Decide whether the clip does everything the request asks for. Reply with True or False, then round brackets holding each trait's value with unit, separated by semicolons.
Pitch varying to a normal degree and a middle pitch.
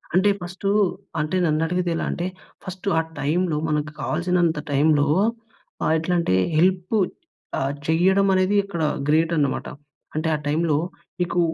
True (3.0 semitones; 170 Hz)